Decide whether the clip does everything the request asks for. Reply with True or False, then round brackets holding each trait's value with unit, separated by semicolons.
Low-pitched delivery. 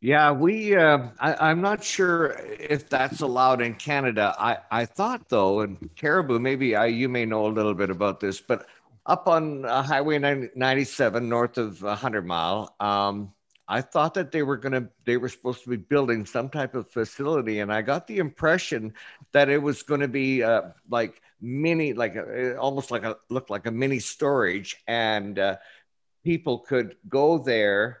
True (130 Hz)